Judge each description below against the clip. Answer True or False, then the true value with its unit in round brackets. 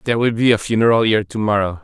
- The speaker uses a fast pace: True (260 wpm)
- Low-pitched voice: True (110 Hz)